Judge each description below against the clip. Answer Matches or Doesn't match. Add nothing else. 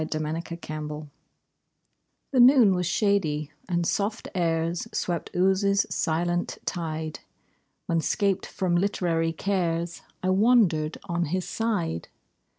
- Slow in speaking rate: Matches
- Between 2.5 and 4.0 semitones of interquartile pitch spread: Matches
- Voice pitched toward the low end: Doesn't match